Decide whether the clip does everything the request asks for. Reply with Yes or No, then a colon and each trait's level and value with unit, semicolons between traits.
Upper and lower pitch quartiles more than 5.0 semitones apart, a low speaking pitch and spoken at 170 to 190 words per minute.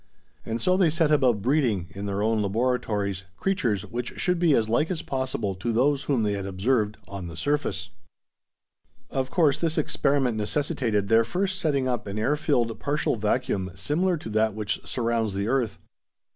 Yes: wide, 5.6 semitones; low, 120 Hz; average, 175 wpm